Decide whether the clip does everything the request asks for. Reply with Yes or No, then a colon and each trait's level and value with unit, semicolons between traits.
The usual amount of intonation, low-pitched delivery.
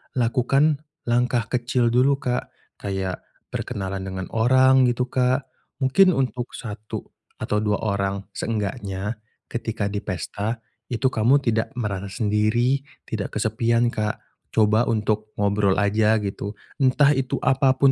Yes: average, 3.6 semitones; low, 115 Hz